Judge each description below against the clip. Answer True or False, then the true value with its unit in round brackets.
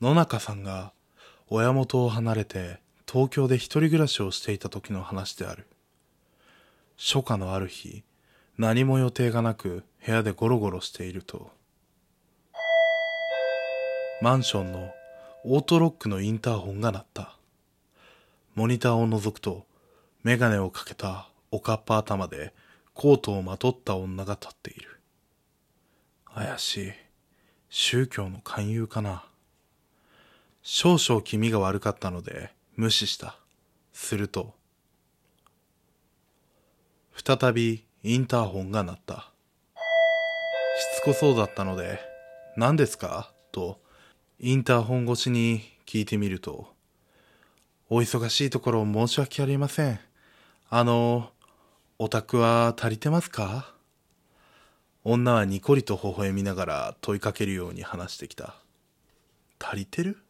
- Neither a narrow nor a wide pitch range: True (4.4 semitones)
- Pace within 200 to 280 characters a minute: True (240 characters per minute)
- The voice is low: True (115 Hz)